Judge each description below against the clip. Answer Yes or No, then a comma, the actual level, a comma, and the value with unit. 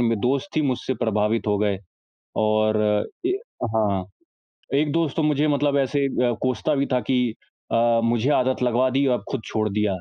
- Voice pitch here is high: No, low, 125 Hz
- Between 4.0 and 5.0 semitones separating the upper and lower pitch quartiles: Yes, average, 4.4 semitones